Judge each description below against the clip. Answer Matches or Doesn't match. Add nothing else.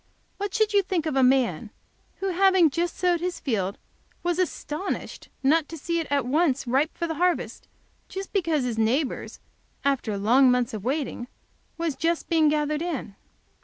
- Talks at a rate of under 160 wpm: Doesn't match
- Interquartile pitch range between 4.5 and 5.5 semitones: Matches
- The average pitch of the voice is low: Doesn't match